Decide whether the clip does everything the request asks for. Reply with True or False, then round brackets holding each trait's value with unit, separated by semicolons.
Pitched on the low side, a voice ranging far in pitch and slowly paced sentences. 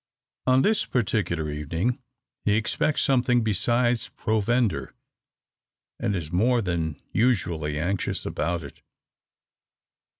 True (105 Hz; 6.3 semitones; 100 wpm)